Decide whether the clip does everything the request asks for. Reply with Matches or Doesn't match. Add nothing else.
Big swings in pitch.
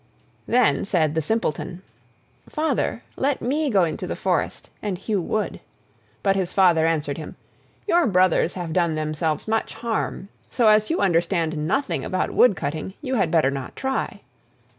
Matches